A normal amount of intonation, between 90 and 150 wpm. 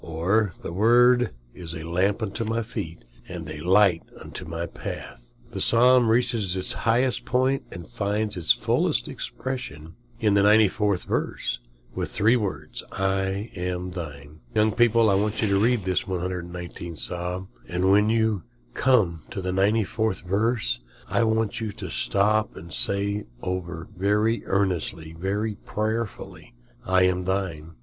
Yes: average, 3.8 semitones; average, 145 wpm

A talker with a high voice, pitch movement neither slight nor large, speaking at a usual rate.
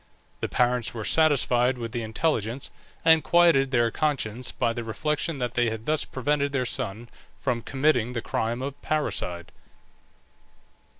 No: low, 125 Hz; average, 4.0 semitones; average, 145 wpm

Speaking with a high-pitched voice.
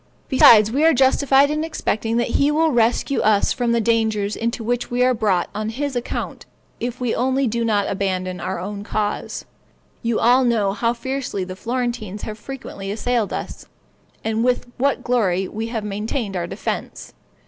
Yes: high, 230 Hz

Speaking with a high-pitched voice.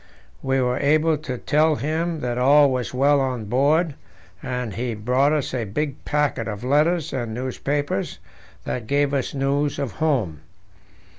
No: low, 135 Hz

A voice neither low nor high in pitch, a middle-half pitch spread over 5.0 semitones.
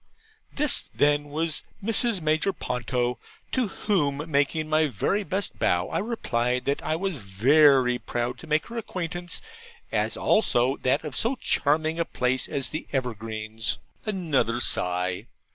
Yes: medium, 145 Hz; wide, 5.5 semitones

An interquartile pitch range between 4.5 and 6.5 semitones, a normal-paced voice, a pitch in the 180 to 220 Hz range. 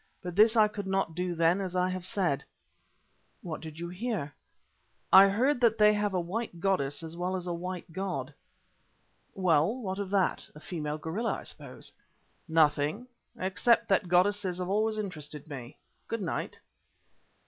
No: average, 3.8 semitones; average, 170 wpm; medium, 185 Hz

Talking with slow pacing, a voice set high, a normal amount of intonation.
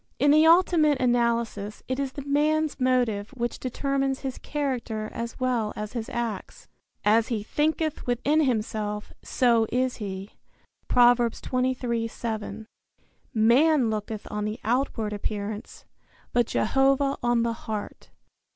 Yes: slow, 125 wpm; high, 240 Hz; average, 3.7 semitones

